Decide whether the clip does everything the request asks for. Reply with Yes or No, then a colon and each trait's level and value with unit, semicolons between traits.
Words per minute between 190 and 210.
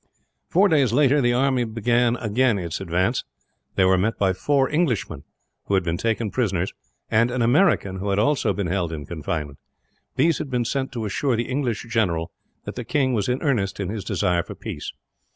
Yes: average, 195 wpm